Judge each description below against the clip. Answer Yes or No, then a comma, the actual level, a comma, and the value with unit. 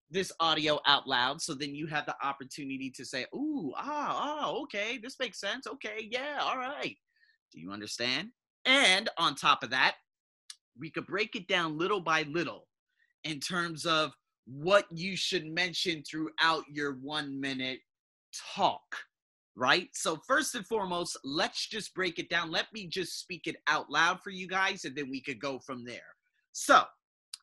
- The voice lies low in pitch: No, medium, 170 Hz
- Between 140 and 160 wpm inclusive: No, average, 175 wpm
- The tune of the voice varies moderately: No, wide, 6.8 semitones